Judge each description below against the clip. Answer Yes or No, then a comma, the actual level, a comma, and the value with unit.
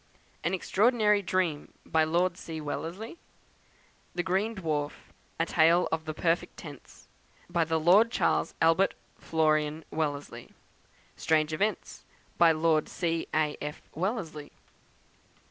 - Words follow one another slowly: Yes, slow, 120 wpm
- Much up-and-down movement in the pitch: No, average, 3.1 semitones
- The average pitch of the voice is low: No, medium, 165 Hz